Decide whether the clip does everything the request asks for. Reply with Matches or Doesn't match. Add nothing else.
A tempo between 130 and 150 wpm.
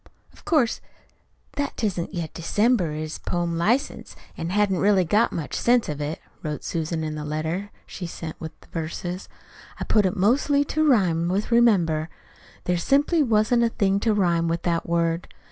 Doesn't match